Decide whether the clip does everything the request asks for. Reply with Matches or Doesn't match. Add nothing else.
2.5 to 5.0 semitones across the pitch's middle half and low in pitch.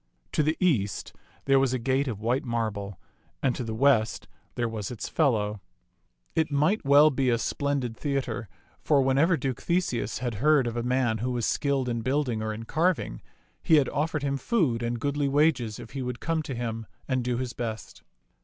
Matches